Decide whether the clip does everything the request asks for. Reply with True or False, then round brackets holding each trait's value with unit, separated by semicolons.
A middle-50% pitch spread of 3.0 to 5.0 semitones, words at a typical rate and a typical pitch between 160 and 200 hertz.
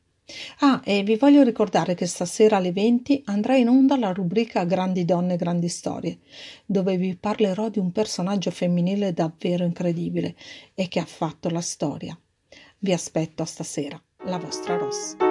True (3.7 semitones; 155 wpm; 185 Hz)